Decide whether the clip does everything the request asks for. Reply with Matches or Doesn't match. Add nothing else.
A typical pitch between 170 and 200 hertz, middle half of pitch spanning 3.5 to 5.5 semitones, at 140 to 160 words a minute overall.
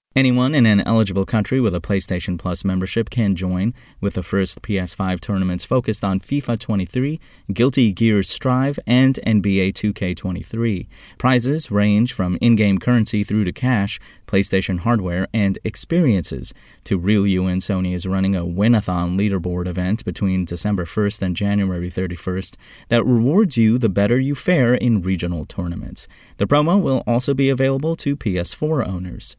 Doesn't match